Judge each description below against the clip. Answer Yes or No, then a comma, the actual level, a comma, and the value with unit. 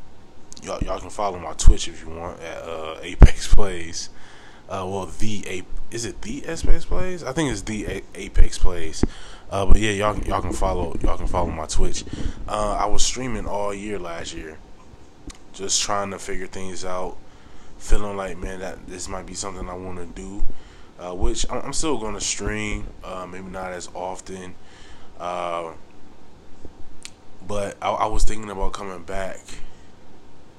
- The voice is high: No, very low, 95 Hz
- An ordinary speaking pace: Yes, average, 170 wpm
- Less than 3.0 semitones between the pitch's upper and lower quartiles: Yes, narrow, 2.5 semitones